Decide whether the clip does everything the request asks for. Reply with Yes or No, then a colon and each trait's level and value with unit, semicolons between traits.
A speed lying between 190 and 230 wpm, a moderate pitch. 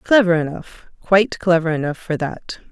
No: slow, 135 wpm; medium, 175 Hz